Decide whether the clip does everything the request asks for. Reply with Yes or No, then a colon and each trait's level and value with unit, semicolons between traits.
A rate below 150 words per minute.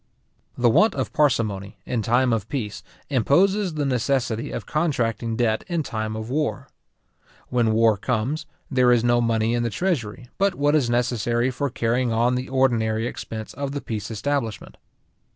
No: average, 165 wpm